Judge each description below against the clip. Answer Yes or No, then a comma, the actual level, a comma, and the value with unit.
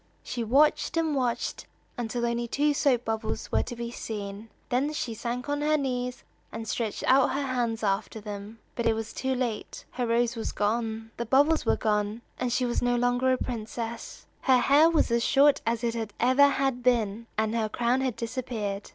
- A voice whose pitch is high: Yes, high, 240 Hz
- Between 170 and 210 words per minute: Yes, average, 195 wpm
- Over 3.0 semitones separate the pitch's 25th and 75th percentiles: No, narrow, 2.5 semitones